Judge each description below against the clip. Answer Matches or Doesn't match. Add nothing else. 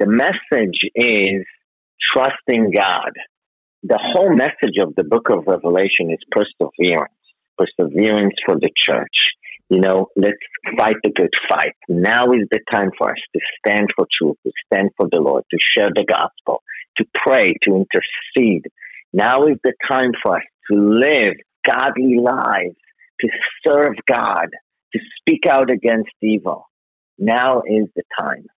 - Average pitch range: Matches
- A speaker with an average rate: Matches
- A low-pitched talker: Matches